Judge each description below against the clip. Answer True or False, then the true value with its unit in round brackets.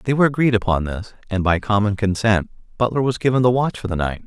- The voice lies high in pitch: False (110 Hz)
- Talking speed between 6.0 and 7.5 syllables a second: True (6.3 syllables/s)